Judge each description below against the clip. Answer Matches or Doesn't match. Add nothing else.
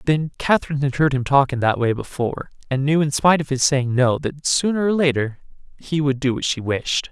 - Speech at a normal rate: Doesn't match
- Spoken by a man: Matches